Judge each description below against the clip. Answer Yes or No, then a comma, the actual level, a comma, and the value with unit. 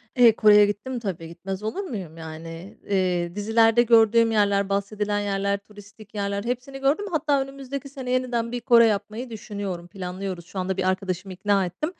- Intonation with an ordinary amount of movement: Yes, average, 3.7 semitones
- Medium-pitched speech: No, high, 205 Hz